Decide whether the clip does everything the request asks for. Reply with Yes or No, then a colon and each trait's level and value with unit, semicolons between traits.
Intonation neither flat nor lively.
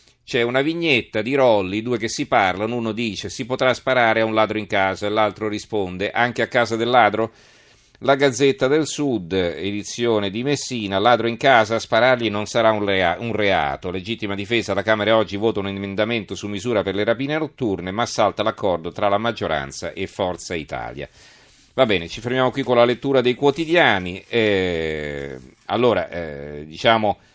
Yes: average, 3.6 semitones